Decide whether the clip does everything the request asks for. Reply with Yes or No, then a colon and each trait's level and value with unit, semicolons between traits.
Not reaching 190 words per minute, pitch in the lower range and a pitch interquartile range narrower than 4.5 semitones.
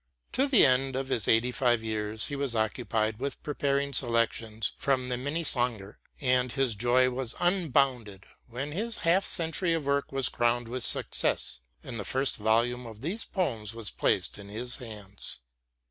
Yes: average, 165 wpm; low, 125 Hz; average, 3.7 semitones